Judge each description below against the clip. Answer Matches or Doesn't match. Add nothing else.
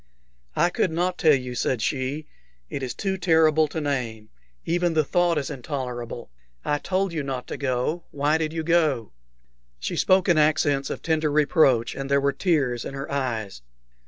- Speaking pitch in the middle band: Matches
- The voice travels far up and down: Doesn't match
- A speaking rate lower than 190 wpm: Matches